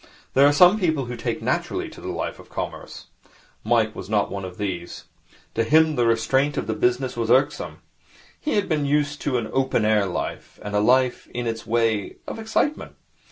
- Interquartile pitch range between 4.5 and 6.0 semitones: Yes, average, 4.8 semitones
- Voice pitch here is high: No, low, 125 Hz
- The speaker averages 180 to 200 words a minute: Yes, average, 195 wpm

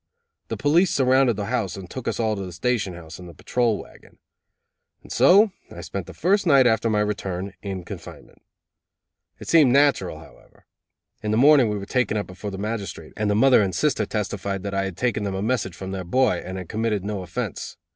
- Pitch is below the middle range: Yes, low, 105 Hz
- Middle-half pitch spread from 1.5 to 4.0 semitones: No, average, 4.6 semitones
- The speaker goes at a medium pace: No, fast, 210 wpm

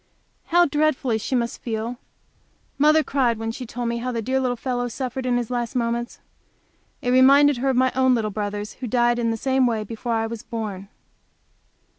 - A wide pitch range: No, narrow, 2.4 semitones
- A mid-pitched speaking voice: No, high, 245 Hz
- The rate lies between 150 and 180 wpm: No, average, 195 wpm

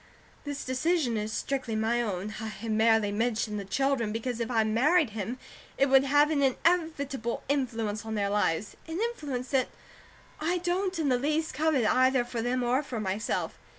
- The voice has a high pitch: Yes, very high, 250 Hz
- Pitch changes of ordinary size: Yes, average, 4.5 semitones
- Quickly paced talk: No, average, 175 wpm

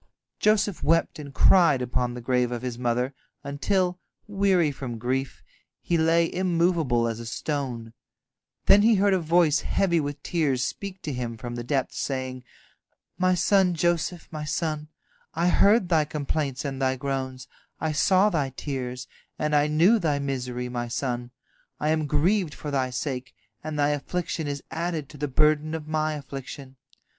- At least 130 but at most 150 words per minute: No, average, 165 wpm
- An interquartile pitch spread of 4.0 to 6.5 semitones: Yes, average, 4.6 semitones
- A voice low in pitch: No, medium, 150 Hz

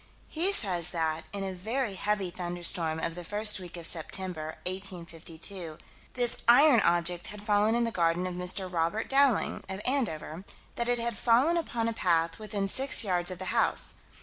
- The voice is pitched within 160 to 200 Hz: Yes, high, 190 Hz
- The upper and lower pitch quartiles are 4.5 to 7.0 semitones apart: Yes, average, 4.8 semitones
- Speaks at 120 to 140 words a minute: No, average, 175 wpm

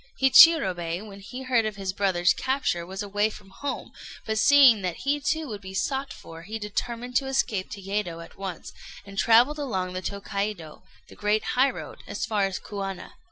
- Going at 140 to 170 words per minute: No, average, 185 wpm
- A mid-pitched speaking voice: No, high, 205 Hz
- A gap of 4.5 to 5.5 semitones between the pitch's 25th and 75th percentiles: Yes, average, 4.8 semitones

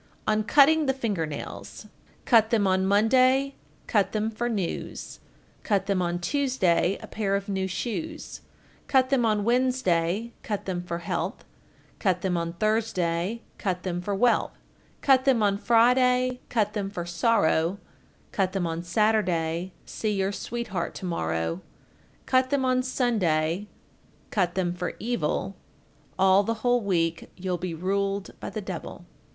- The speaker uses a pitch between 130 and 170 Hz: No, high, 200 Hz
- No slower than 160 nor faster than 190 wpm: No, average, 150 wpm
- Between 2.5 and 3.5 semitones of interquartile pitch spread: No, average, 5.0 semitones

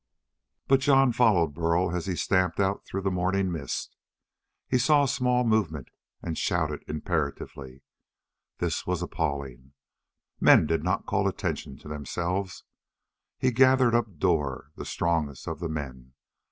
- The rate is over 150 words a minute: No, average, 140 wpm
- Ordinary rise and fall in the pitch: Yes, average, 5.0 semitones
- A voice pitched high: No, very low, 85 Hz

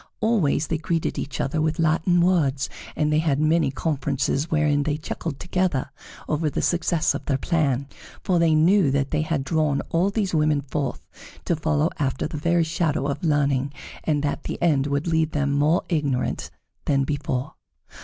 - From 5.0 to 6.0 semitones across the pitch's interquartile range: No, average, 2.7 semitones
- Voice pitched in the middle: Yes, medium, 155 Hz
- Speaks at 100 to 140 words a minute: No, average, 175 wpm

